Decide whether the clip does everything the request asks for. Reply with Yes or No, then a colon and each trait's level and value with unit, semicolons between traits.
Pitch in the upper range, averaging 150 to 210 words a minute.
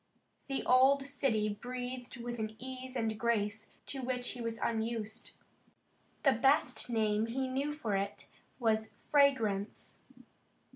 No: high, 240 Hz; slow, 135 wpm